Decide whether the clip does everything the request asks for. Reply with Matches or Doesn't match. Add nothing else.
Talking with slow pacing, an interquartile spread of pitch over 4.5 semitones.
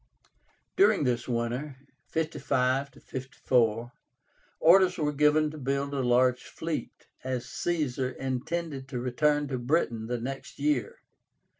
Doesn't match